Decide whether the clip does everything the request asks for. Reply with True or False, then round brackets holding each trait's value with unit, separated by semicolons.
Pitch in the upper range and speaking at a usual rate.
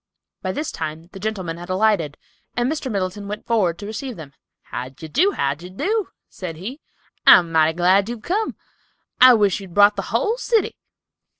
True (200 Hz; 185 wpm)